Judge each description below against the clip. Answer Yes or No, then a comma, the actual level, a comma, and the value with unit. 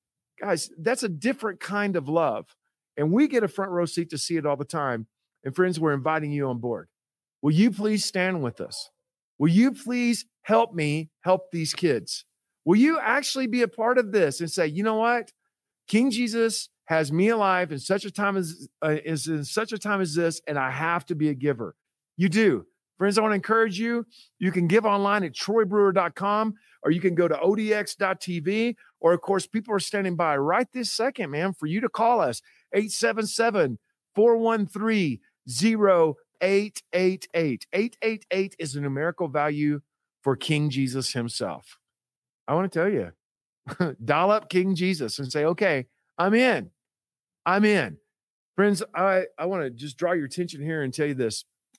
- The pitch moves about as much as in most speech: No, wide, 5.9 semitones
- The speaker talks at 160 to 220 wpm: Yes, average, 180 wpm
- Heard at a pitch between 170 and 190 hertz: Yes, medium, 185 Hz